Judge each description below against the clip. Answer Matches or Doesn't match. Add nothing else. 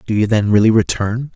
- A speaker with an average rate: Doesn't match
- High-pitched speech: Doesn't match